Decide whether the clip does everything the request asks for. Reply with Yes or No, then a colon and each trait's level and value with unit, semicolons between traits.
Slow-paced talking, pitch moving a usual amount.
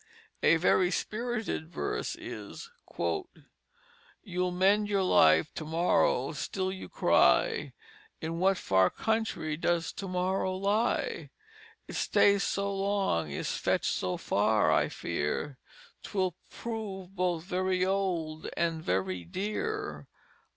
Yes: slow, 115 wpm; average, 3.7 semitones